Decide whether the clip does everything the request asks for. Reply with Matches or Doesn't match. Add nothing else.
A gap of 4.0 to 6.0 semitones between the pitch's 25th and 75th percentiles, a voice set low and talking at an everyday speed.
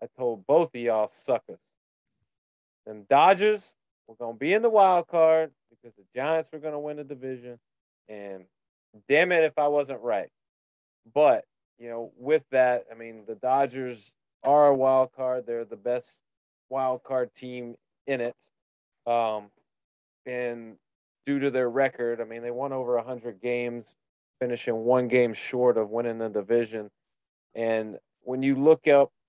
Doesn't match